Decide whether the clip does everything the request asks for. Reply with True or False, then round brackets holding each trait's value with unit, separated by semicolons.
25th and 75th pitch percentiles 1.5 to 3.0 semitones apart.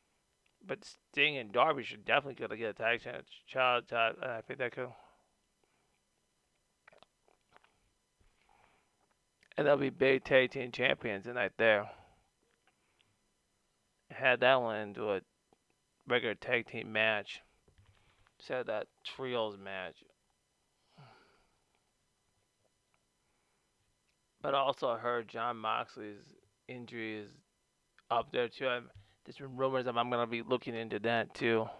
True (2.7 semitones)